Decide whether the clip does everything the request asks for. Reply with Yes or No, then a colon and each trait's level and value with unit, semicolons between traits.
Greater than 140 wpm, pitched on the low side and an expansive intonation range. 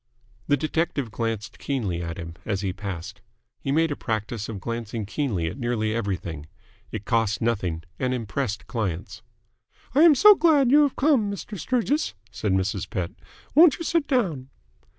Yes: average, 165 wpm; low, 115 Hz; wide, 8.9 semitones